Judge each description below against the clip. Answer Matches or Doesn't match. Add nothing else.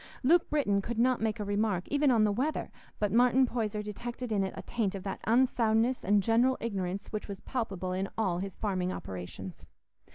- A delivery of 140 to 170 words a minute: Doesn't match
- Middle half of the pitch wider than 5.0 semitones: Doesn't match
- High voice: Matches